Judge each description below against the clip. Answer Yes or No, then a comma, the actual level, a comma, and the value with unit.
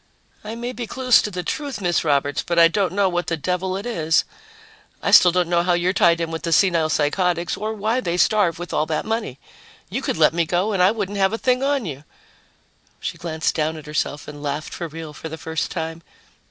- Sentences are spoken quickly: Yes, fast, 235 wpm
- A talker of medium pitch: Yes, medium, 175 Hz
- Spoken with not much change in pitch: No, average, 4.1 semitones